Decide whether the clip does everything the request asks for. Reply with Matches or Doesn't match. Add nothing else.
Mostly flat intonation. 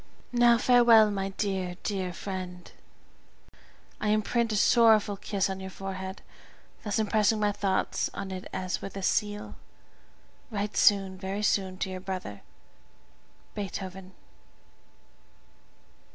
Matches